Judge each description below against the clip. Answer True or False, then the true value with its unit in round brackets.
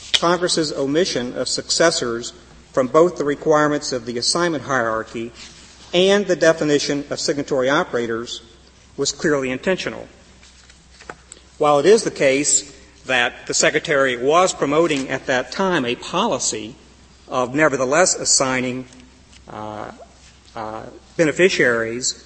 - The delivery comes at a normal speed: False (115 wpm)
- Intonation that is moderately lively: False (5.8 semitones)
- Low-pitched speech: True (130 Hz)